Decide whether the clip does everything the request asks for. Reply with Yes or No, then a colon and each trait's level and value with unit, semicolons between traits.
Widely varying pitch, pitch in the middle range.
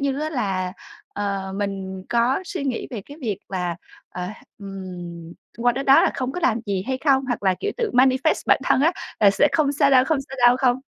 No: wide, 6.0 semitones; high, 245 Hz